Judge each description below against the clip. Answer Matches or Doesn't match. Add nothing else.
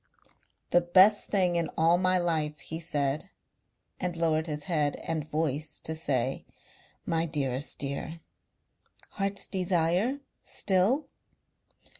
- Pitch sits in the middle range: Matches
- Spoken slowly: Matches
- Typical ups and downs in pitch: Matches